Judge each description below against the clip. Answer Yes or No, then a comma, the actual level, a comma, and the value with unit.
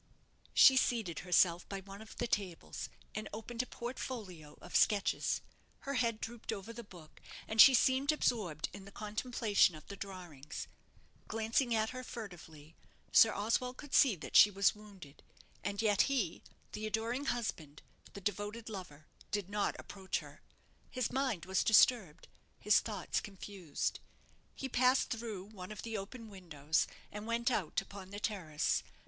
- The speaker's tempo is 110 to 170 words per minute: Yes, average, 155 wpm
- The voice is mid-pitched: No, high, 210 Hz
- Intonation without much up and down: No, average, 3.9 semitones